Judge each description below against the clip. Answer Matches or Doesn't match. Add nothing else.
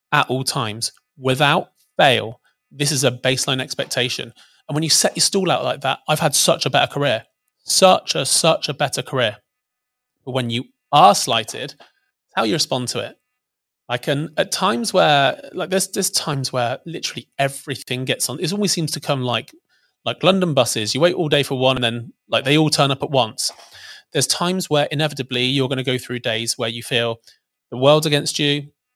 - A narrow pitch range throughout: Doesn't match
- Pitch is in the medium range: Matches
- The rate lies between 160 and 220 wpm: Matches